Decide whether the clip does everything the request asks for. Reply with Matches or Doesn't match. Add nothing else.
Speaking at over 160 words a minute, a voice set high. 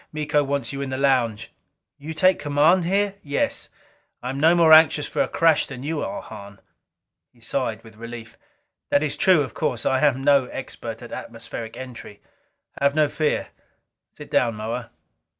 Doesn't match